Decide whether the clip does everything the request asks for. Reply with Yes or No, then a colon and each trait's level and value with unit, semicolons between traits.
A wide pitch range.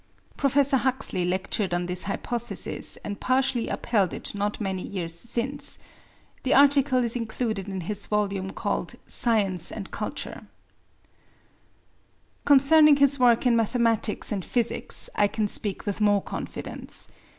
No: average, 4.6 semitones